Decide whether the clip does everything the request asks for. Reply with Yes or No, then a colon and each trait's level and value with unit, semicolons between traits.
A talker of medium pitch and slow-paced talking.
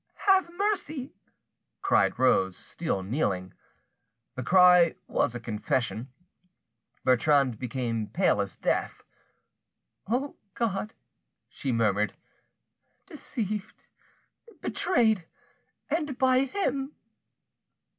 Yes: medium, 170 Hz; slow, 80 wpm